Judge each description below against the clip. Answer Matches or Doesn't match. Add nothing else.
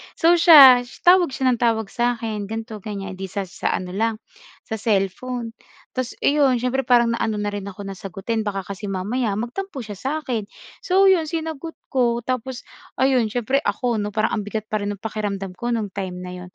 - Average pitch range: Matches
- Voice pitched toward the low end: Doesn't match